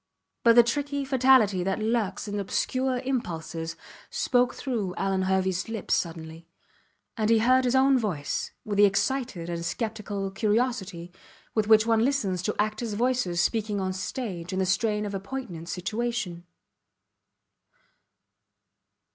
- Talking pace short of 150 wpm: Yes, average, 140 wpm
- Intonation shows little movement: No, average, 4.4 semitones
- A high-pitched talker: Yes, high, 210 Hz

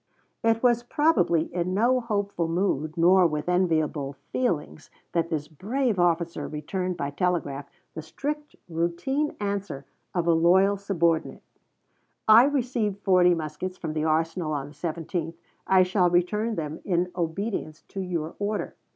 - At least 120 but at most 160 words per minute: Yes, average, 140 wpm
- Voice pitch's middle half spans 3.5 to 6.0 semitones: Yes, average, 4.0 semitones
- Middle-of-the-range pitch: Yes, medium, 180 Hz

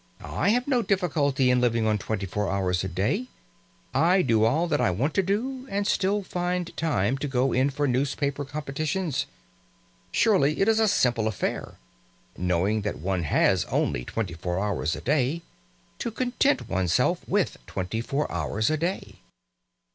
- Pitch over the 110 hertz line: Yes, low, 135 Hz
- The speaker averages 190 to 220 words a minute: No, average, 170 wpm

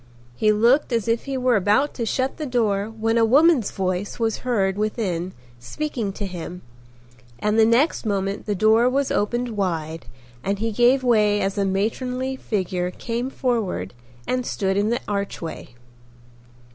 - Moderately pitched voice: No, high, 220 Hz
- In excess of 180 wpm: No, average, 160 wpm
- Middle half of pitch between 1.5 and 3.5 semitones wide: No, average, 3.9 semitones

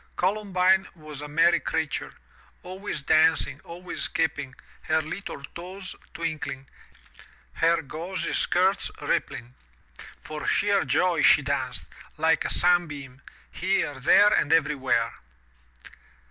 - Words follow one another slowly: Yes, slow, 110 wpm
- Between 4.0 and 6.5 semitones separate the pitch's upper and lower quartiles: No, average, 3.6 semitones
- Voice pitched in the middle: Yes, medium, 165 Hz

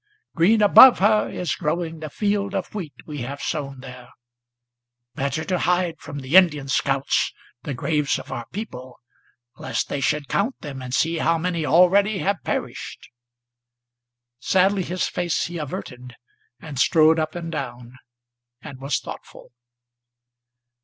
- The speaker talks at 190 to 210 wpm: No, average, 145 wpm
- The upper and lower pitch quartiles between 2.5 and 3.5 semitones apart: No, average, 4.9 semitones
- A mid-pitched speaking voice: Yes, medium, 160 Hz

